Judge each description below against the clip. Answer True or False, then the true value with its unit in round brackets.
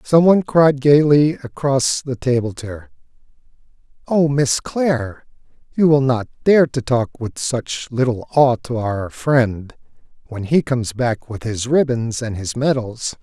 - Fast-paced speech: False (155 wpm)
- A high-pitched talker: False (130 Hz)